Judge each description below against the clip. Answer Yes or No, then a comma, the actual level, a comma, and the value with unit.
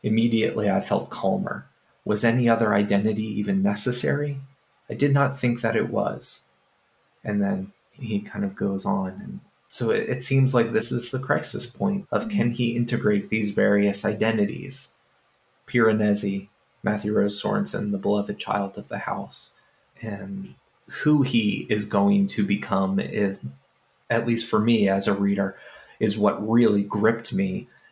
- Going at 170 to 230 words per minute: No, average, 155 wpm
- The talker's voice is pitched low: Yes, low, 115 Hz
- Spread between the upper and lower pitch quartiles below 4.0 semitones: No, average, 5.3 semitones